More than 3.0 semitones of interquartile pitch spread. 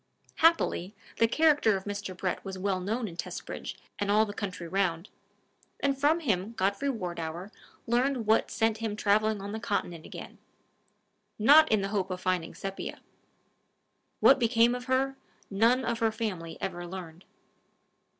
Yes: average, 4.0 semitones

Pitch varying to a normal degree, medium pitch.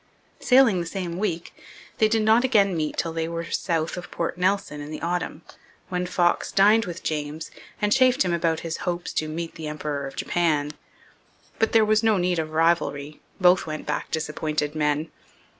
Yes: average, 3.9 semitones; medium, 170 Hz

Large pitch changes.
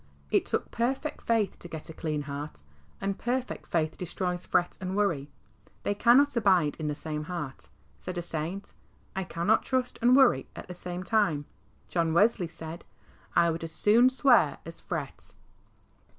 Yes: wide, 5.7 semitones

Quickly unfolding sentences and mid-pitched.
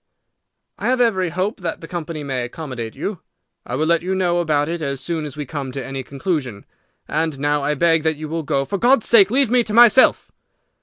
Yes: fast, 220 wpm; medium, 160 Hz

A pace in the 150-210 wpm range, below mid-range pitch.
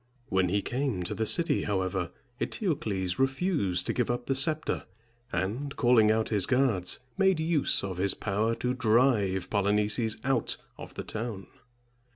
Yes: average, 155 wpm; low, 110 Hz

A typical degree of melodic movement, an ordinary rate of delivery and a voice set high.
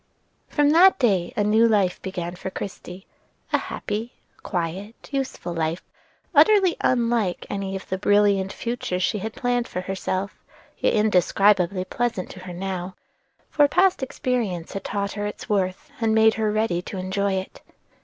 Yes: average, 3.8 semitones; average, 155 wpm; high, 200 Hz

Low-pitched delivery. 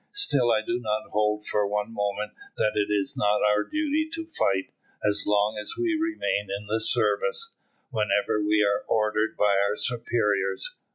Yes: low, 105 Hz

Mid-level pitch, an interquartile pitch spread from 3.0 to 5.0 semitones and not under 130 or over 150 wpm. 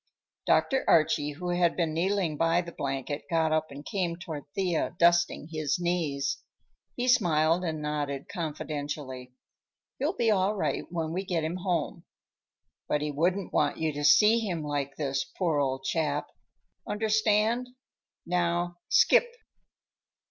Yes: medium, 165 Hz; average, 3.6 semitones; average, 140 wpm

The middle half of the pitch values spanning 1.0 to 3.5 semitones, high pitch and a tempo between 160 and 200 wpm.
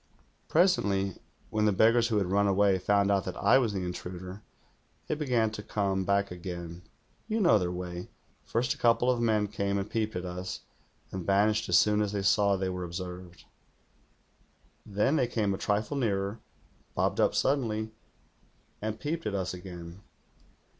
No: average, 2.9 semitones; low, 100 Hz; average, 170 wpm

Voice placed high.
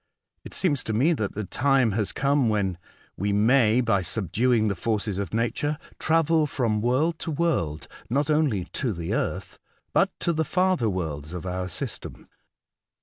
No: low, 115 Hz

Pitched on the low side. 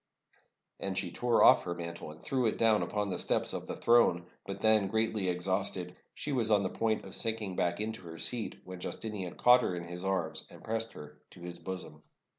Yes: very low, 95 Hz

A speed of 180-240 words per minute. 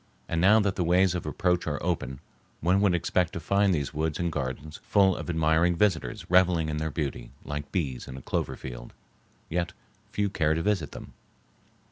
Yes: average, 190 wpm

